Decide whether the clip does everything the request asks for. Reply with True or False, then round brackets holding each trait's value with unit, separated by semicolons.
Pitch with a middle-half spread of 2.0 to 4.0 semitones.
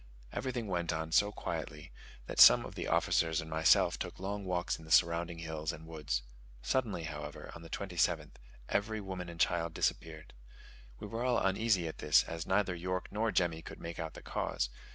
True (3.3 semitones)